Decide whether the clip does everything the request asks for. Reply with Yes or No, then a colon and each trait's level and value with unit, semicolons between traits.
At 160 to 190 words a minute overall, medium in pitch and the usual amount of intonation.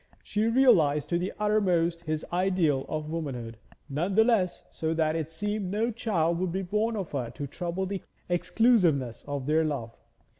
Yes: average, 175 wpm; medium, 170 Hz; average, 4.8 semitones